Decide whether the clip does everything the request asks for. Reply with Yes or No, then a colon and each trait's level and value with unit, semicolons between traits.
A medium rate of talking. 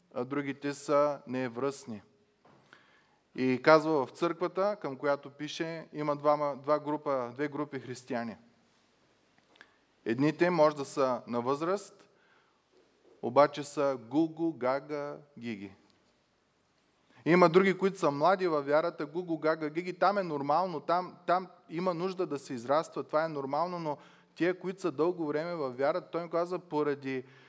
Yes: average, 140 wpm